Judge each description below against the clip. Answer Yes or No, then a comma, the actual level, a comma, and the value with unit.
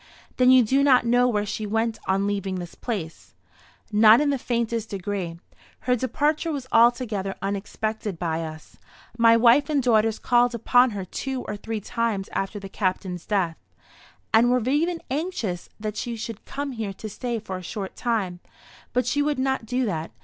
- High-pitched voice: Yes, high, 225 Hz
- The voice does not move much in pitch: No, average, 4.1 semitones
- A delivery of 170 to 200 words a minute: Yes, average, 180 wpm